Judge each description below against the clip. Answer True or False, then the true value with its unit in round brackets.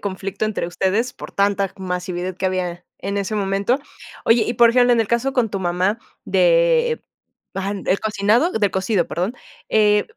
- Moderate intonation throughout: True (3.7 semitones)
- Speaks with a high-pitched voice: True (200 Hz)